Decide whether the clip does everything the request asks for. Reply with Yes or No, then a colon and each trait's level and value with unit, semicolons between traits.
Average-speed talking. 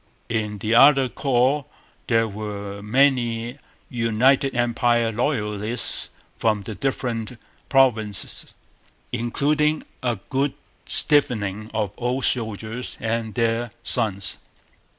No: slow, 95 wpm